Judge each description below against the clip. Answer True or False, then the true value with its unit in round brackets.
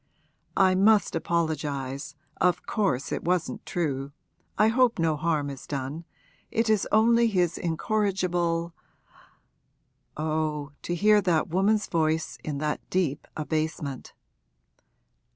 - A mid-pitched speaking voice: True (165 Hz)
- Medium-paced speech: False (115 wpm)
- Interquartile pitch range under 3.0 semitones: False (4.3 semitones)